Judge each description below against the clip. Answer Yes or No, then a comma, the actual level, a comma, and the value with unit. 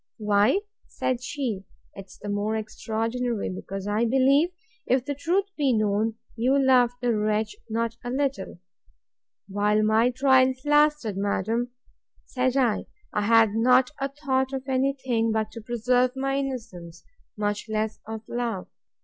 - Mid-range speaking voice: No, high, 235 Hz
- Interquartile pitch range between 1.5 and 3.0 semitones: No, average, 3.6 semitones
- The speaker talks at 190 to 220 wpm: No, average, 145 wpm